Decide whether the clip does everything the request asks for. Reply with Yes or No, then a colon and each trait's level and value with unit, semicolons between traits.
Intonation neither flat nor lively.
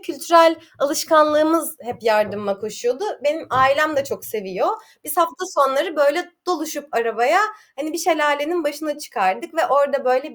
Yes: average, 3.6 semitones